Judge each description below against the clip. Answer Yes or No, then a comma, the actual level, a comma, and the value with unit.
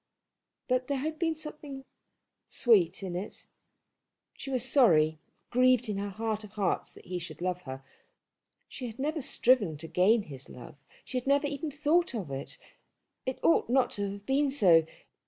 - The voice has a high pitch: Yes, high, 225 Hz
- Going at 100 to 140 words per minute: No, average, 175 wpm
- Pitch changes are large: Yes, wide, 7.1 semitones